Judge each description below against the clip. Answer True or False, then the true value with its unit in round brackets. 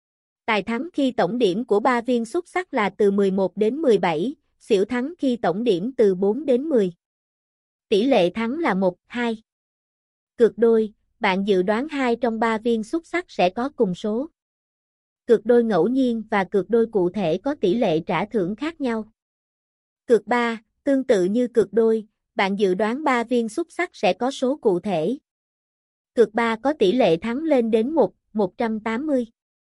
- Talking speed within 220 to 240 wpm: False (180 wpm)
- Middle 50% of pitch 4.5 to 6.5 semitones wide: False (3.5 semitones)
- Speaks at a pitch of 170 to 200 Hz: False (230 Hz)